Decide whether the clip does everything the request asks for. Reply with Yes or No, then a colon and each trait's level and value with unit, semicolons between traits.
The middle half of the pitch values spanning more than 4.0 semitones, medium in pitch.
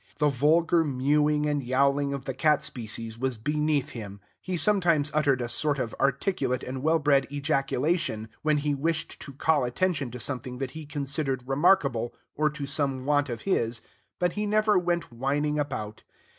No: average, 3.0 semitones; medium, 145 Hz